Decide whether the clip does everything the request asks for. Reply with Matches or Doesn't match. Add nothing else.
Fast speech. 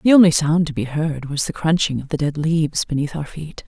Matches